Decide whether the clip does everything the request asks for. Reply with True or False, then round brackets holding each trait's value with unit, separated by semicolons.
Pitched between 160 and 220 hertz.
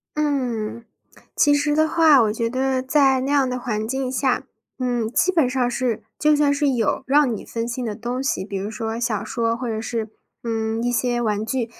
False (245 Hz)